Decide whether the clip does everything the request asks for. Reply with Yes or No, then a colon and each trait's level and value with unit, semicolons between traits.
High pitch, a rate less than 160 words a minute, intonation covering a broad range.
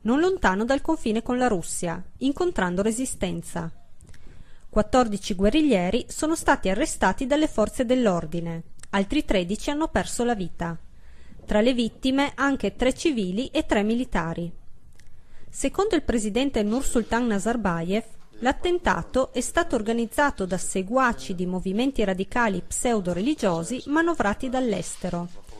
Yes: high, 225 Hz; slow, 115 wpm; wide, 5.9 semitones